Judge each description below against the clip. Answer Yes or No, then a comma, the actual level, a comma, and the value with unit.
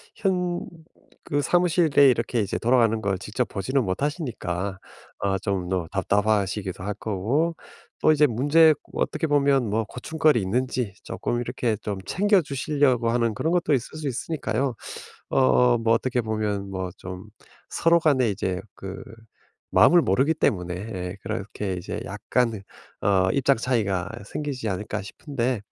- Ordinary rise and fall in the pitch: No, wide, 6.2 semitones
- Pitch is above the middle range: No, low, 115 Hz